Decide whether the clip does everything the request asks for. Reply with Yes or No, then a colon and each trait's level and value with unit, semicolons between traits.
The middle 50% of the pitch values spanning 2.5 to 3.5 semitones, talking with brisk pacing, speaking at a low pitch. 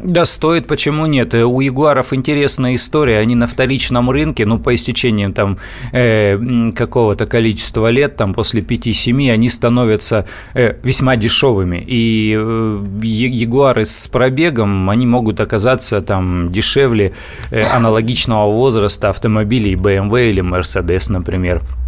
No: average, 3.2 semitones; average, 125 wpm; low, 115 Hz